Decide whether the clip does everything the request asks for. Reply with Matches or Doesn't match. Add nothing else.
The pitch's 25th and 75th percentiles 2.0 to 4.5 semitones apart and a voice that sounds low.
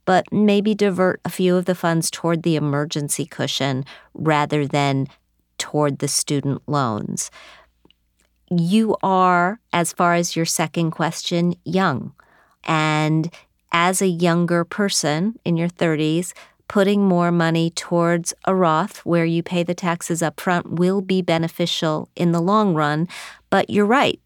Doesn't match